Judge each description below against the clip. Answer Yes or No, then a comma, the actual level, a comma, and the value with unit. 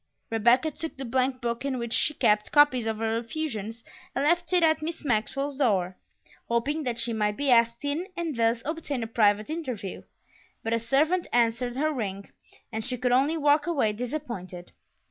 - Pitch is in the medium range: No, high, 245 Hz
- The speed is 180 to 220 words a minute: Yes, average, 185 wpm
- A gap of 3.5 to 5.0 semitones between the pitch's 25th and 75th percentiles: Yes, average, 4.5 semitones